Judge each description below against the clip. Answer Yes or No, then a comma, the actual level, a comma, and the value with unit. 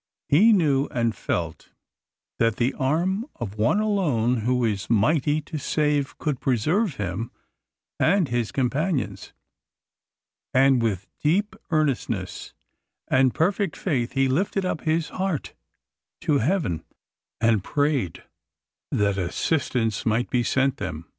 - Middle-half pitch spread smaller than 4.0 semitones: No, wide, 5.6 semitones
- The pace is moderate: No, slow, 120 wpm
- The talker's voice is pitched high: No, low, 135 Hz